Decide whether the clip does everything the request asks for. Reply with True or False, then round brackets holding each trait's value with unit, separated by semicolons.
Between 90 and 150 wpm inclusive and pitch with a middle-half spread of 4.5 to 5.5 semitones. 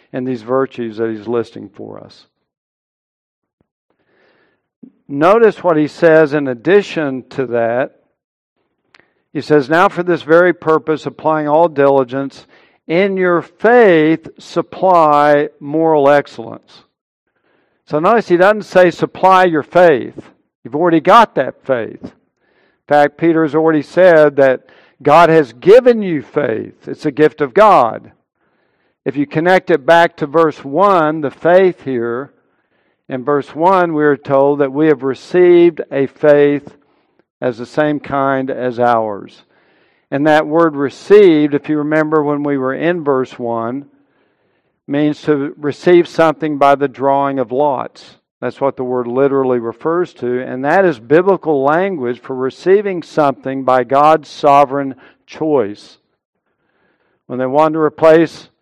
False (140 wpm; 3.6 semitones)